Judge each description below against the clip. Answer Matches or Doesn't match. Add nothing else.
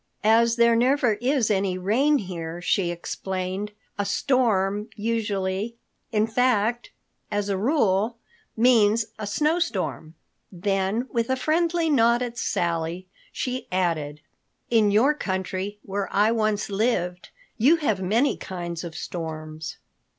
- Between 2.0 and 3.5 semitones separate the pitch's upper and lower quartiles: Doesn't match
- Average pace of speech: Doesn't match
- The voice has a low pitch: Doesn't match